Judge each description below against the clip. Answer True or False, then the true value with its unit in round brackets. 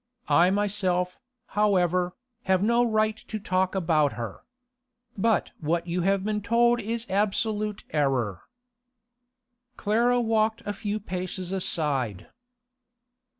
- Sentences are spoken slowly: True (110 wpm)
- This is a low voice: False (195 Hz)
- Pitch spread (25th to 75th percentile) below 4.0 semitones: True (3.5 semitones)